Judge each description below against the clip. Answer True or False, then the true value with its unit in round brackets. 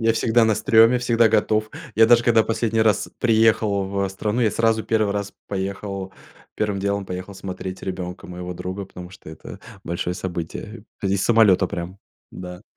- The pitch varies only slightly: False (3.2 semitones)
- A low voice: True (100 Hz)